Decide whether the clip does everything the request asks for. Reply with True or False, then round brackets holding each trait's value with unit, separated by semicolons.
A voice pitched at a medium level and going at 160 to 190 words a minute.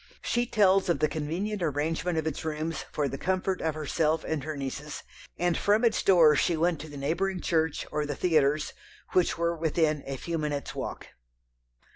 True (160 Hz; 185 wpm)